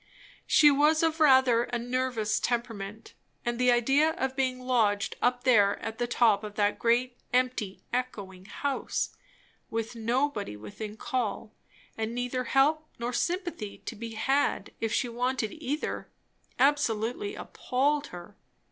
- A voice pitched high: Yes, high, 245 Hz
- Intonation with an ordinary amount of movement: Yes, average, 3.2 semitones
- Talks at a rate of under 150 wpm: Yes, average, 140 wpm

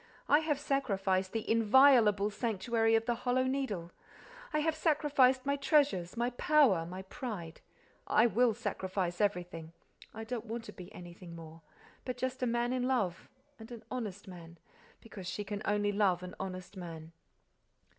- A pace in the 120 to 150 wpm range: Yes, average, 145 wpm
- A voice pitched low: No, high, 220 Hz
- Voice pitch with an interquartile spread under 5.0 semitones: No, wide, 5.5 semitones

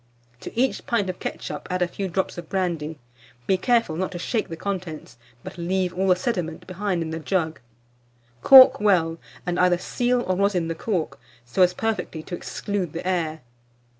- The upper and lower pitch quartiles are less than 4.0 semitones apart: Yes, average, 3.1 semitones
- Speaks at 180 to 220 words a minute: Yes, average, 185 wpm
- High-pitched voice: No, medium, 180 Hz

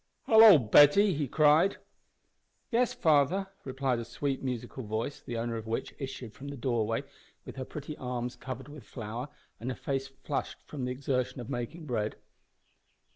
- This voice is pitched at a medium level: No, low, 130 Hz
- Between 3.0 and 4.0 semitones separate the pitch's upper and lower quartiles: Yes, average, 3.5 semitones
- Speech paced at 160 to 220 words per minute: Yes, average, 165 wpm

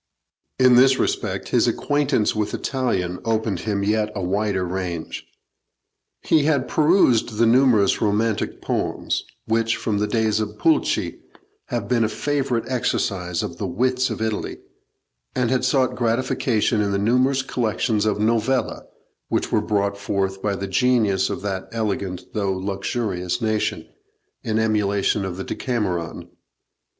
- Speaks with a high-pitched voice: No, low, 110 Hz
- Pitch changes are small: No, average, 3.8 semitones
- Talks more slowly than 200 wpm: Yes, average, 140 wpm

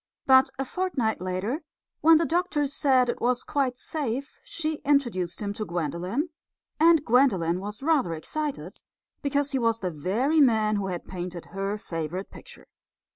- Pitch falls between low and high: No, high, 245 Hz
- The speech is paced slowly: No, average, 160 wpm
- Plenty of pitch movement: Yes, wide, 7.3 semitones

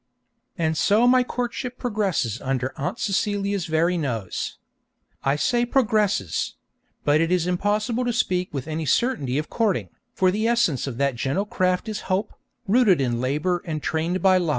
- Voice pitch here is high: No, medium, 180 Hz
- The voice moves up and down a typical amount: No, wide, 6.4 semitones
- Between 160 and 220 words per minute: Yes, average, 165 wpm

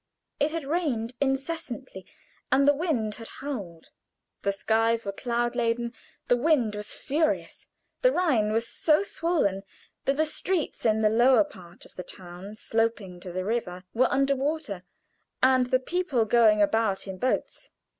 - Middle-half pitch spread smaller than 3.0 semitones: No, average, 5.0 semitones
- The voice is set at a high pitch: Yes, high, 235 Hz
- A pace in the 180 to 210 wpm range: No, average, 155 wpm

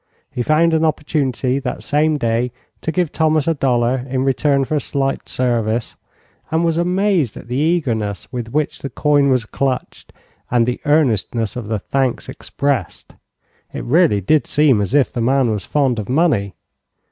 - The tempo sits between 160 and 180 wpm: Yes, average, 170 wpm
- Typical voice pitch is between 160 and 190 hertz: No, low, 135 Hz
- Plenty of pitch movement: No, average, 4.4 semitones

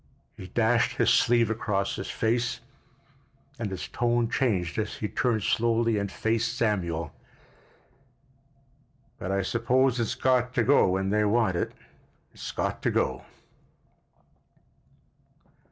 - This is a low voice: Yes, low, 115 Hz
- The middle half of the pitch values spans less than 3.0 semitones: No, average, 3.5 semitones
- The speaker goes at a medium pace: No, slow, 120 wpm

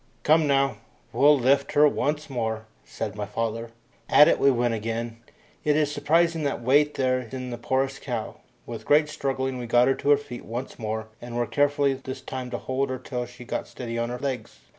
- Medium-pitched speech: No, low, 130 Hz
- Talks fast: Yes, fast, 210 wpm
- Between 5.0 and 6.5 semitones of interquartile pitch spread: No, average, 3.2 semitones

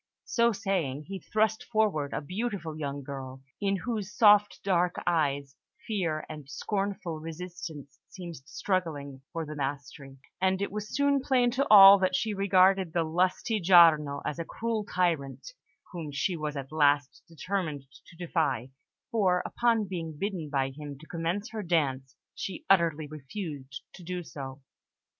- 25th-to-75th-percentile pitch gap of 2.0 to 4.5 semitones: No, average, 5.2 semitones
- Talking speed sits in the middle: Yes, average, 150 wpm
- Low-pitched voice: No, medium, 170 Hz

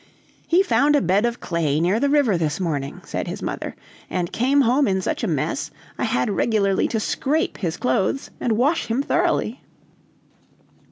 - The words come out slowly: No, average, 175 wpm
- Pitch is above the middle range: Yes, high, 215 Hz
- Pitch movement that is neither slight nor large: No, wide, 7.9 semitones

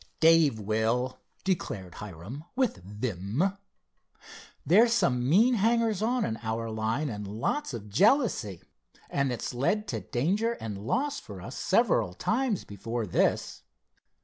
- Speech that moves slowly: Yes, slow, 130 wpm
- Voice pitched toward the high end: No, low, 130 Hz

